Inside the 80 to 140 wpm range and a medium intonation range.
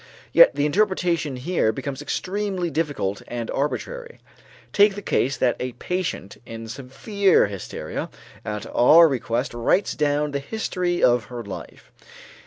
No: slow, 135 wpm; wide, 7.1 semitones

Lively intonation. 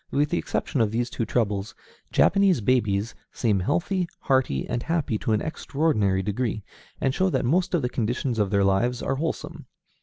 Yes: wide, 6.0 semitones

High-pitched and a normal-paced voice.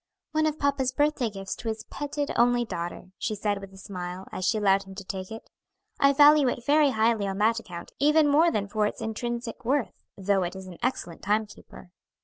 No: high, 220 Hz; fast, 215 wpm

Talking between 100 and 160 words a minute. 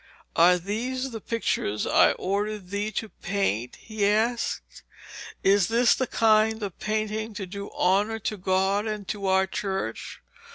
Yes: average, 150 wpm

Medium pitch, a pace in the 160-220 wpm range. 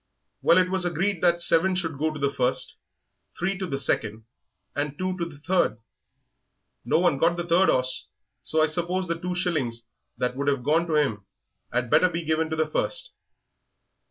Yes: medium, 160 Hz; average, 190 wpm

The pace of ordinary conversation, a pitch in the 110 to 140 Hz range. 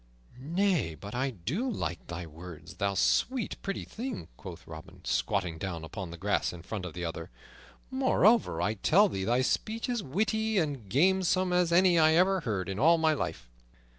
Yes: average, 180 wpm; low, 135 Hz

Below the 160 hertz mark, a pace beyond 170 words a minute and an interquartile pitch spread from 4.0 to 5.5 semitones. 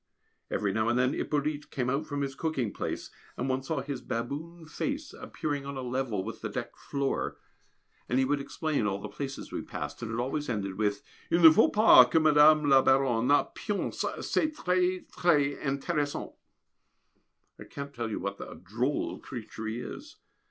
Yes: low, 135 Hz; average, 180 wpm; average, 4.3 semitones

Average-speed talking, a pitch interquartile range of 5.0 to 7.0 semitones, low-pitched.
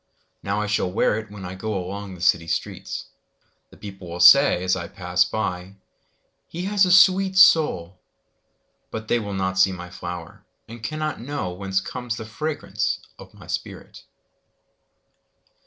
No: slow, 125 wpm; average, 5.3 semitones; low, 100 Hz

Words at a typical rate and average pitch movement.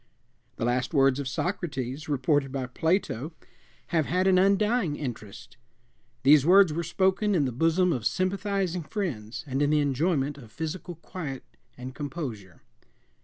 No: average, 145 wpm; wide, 5.8 semitones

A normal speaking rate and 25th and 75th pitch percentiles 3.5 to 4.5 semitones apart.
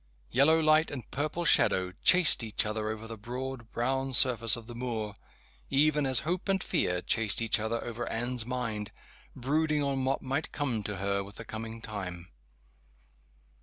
Yes: average, 165 wpm; average, 4.1 semitones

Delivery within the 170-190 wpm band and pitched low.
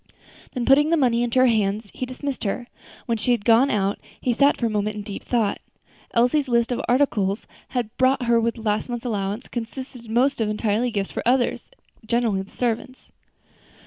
No: average, 185 wpm; high, 235 Hz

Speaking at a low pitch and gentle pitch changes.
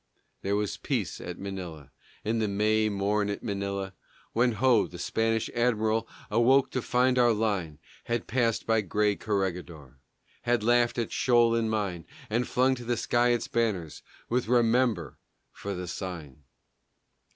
No: low, 110 Hz; average, 3.4 semitones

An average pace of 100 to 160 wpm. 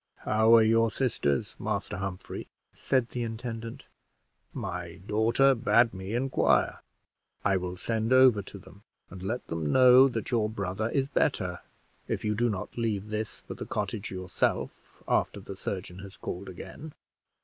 Yes: average, 155 wpm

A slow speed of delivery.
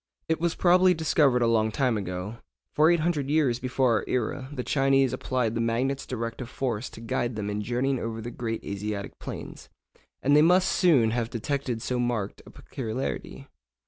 No: average, 175 wpm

